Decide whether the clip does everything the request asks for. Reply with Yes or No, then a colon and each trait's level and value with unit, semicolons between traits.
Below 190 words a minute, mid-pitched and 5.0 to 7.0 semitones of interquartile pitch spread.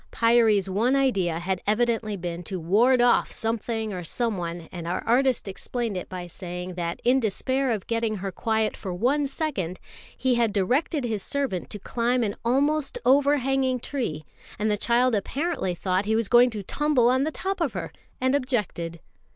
No: average, 175 wpm; high, 225 Hz; wide, 5.4 semitones